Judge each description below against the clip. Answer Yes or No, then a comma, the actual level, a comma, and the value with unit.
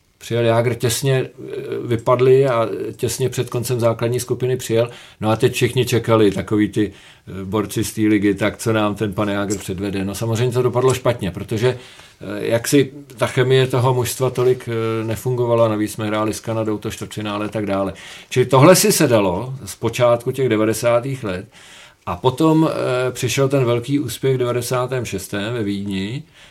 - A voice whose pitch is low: Yes, low, 120 Hz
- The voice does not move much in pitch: No, average, 3.0 semitones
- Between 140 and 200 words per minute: Yes, average, 165 wpm